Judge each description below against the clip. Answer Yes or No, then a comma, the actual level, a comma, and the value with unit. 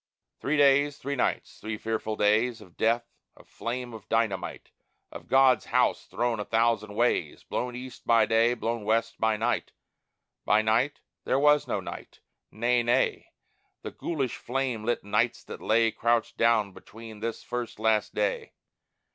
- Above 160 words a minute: No, average, 155 wpm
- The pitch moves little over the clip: Yes, narrow, 2.0 semitones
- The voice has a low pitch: Yes, low, 115 Hz